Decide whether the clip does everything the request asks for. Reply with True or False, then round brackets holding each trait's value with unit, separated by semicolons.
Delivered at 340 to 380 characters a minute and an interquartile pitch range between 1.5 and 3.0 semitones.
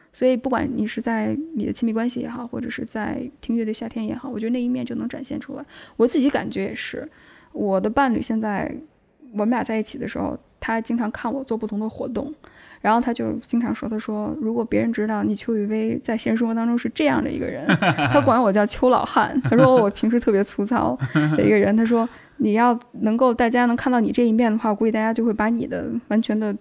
True (345 characters per minute; 2.4 semitones)